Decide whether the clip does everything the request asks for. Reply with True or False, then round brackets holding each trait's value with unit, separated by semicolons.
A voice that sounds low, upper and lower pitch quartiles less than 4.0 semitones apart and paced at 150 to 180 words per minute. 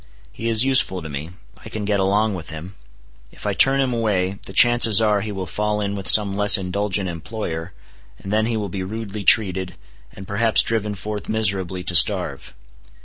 False (100 Hz; 2.7 semitones; 195 wpm)